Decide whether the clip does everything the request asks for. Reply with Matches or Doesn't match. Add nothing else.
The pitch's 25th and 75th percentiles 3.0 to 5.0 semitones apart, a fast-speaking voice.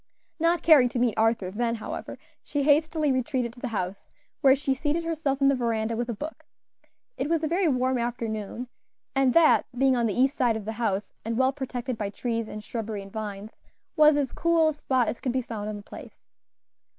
Matches